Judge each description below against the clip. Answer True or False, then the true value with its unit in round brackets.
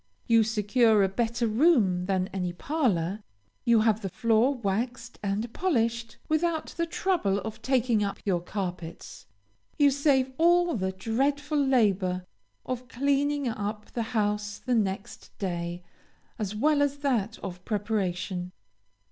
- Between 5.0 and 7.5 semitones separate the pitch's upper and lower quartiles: True (5.3 semitones)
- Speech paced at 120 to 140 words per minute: True (135 wpm)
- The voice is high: True (225 Hz)